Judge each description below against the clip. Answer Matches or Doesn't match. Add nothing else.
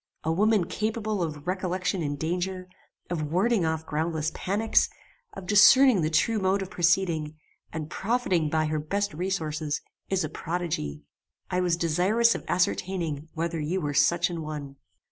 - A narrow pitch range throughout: Doesn't match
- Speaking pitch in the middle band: Matches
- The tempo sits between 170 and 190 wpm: Doesn't match